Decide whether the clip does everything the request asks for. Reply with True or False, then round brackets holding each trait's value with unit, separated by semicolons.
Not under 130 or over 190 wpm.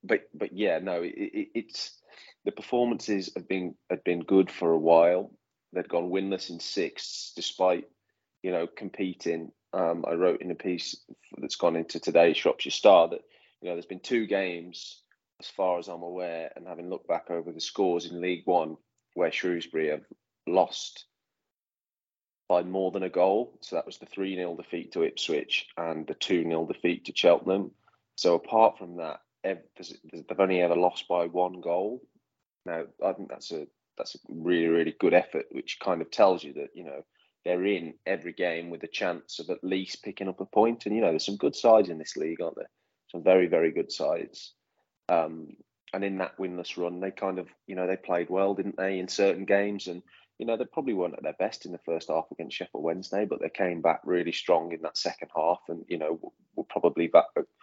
False (205 wpm)